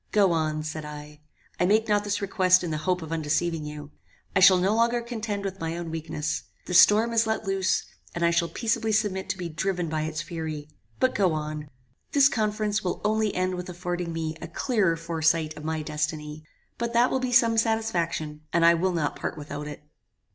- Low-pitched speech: No, medium, 175 Hz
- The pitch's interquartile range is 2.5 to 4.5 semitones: No, average, 5.0 semitones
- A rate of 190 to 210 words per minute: Yes, fast, 205 wpm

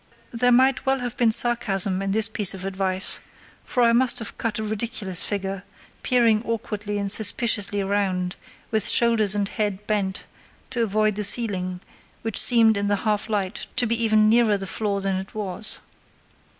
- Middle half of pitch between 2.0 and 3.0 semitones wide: Yes, average, 2.7 semitones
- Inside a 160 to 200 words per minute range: Yes, average, 175 wpm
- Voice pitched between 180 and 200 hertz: No, high, 210 Hz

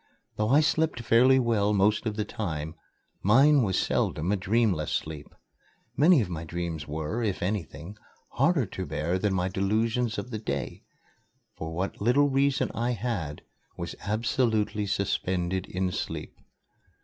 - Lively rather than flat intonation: No, average, 4.7 semitones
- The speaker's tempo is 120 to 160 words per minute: Yes, average, 150 wpm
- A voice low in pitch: Yes, low, 105 Hz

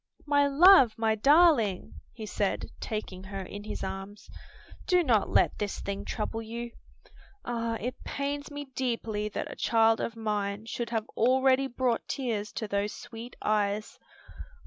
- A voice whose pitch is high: Yes, high, 225 Hz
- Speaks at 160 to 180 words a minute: No, average, 150 wpm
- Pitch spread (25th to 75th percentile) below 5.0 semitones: Yes, average, 3.8 semitones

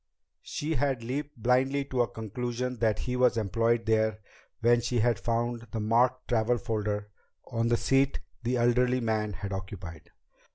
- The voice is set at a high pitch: No, low, 120 Hz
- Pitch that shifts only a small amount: Yes, narrow, 2.3 semitones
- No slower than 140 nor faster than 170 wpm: Yes, average, 160 wpm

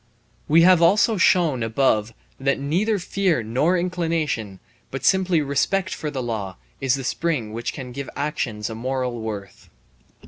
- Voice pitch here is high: No, medium, 140 Hz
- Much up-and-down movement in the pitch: Yes, wide, 6.4 semitones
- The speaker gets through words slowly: No, average, 150 wpm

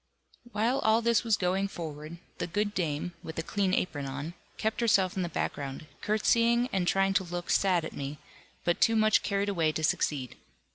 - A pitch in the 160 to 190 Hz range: Yes, medium, 185 Hz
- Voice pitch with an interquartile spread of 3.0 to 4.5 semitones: No, average, 4.9 semitones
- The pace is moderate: Yes, average, 190 wpm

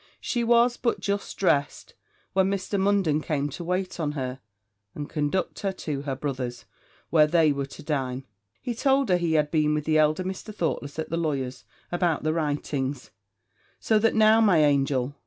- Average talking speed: Yes, average, 180 wpm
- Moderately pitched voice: Yes, medium, 155 Hz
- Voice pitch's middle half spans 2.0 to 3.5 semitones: No, average, 4.9 semitones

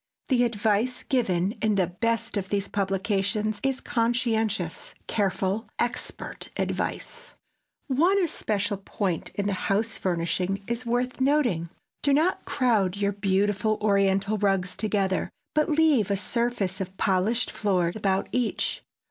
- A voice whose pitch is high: Yes, high, 205 Hz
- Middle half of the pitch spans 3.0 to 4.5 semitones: Yes, average, 3.8 semitones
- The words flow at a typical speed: No, slow, 125 wpm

